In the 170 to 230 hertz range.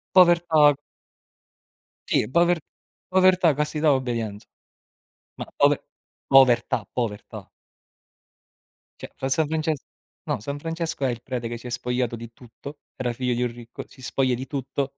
No: low, 135 Hz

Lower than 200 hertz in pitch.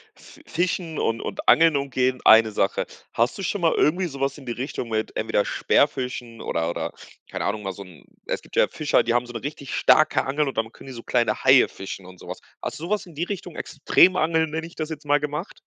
Yes: medium, 140 Hz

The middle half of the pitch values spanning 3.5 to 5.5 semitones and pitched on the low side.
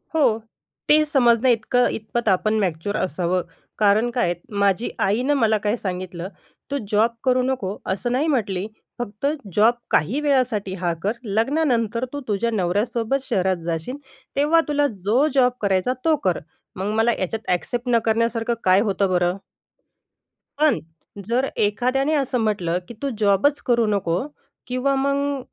No: average, 4.5 semitones; high, 225 Hz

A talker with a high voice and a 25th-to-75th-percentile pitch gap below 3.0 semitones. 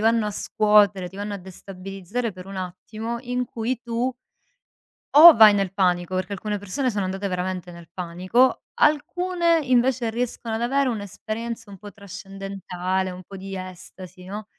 No: high, 205 Hz; average, 4.0 semitones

